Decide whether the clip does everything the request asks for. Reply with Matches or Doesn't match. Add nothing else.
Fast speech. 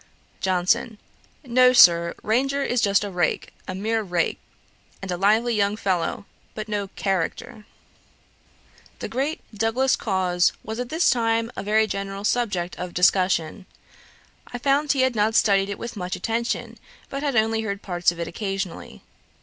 Doesn't match